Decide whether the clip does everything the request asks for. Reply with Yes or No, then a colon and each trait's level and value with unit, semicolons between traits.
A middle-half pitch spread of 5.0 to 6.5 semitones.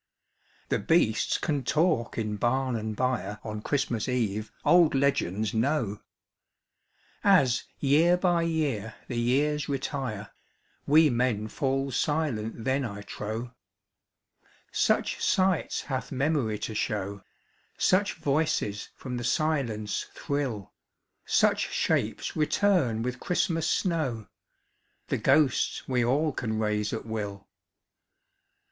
Yes: wide, 5.5 semitones